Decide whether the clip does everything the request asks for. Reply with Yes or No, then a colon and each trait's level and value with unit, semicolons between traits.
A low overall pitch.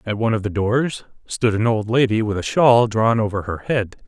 Yes: low, 110 Hz